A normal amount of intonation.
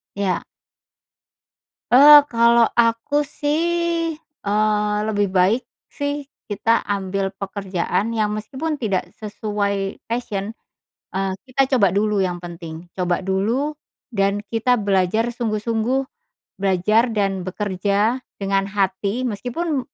Yes: average, 3.3 semitones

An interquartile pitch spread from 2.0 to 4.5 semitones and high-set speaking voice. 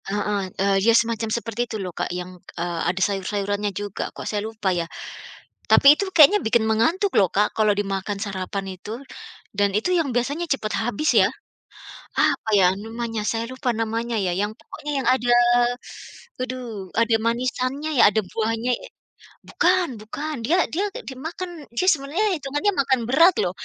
No: average, 5.3 semitones; high, 225 Hz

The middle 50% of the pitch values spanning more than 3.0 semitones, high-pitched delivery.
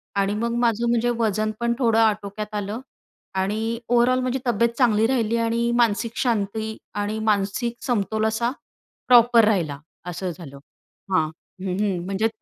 No: average, 2.7 semitones; high, 220 Hz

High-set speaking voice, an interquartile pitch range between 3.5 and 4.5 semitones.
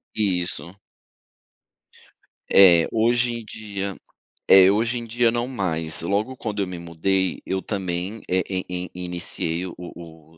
No: very low, 95 Hz; average, 3.9 semitones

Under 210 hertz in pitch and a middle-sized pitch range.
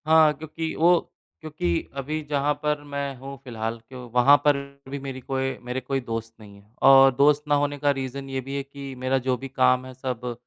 No: low, 135 Hz; narrow, 2.3 semitones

